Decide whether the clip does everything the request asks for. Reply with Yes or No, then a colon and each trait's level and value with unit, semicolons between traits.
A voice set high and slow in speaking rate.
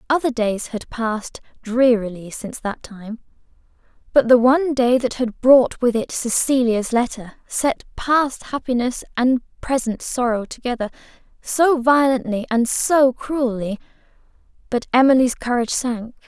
Yes: high, 245 Hz; slow, 130 wpm